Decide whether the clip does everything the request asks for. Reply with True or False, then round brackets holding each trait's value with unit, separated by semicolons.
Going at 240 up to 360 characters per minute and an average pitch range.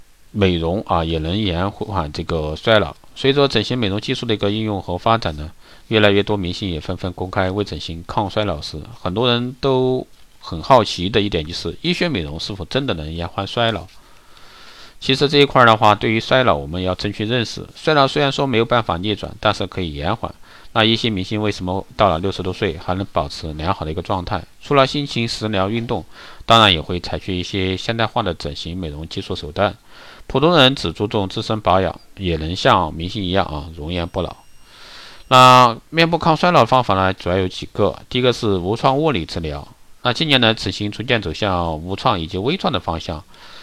True (310 characters per minute; 4.8 semitones)